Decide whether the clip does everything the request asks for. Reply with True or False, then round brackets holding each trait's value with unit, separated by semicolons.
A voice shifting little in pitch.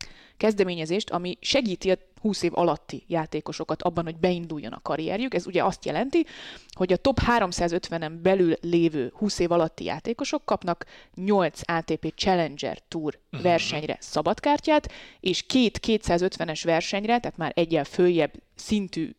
False (3.9 semitones)